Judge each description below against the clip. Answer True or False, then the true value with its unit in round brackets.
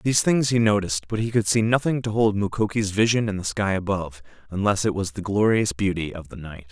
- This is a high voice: False (100 Hz)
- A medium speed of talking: False (230 wpm)